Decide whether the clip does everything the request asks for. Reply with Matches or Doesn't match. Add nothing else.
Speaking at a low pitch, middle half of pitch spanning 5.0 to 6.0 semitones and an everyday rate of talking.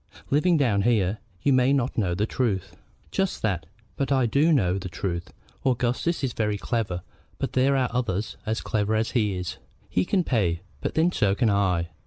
Matches